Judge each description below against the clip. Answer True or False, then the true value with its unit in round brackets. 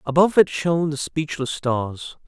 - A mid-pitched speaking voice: True (150 Hz)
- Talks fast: False (160 wpm)